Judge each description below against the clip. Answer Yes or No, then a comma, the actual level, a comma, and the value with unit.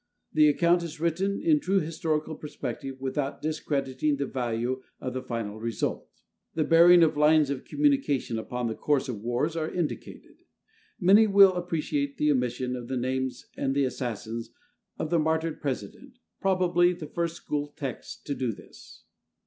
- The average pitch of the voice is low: No, medium, 150 Hz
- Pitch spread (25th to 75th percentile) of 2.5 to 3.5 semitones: No, average, 4.8 semitones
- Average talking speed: Yes, average, 160 wpm